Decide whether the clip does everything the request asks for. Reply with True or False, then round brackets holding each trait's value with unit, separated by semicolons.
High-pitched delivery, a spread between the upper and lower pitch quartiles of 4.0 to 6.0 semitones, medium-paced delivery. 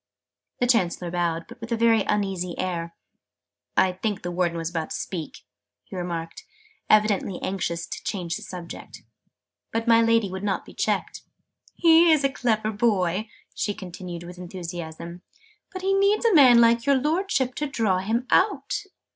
True (200 Hz; 5.2 semitones; 165 wpm)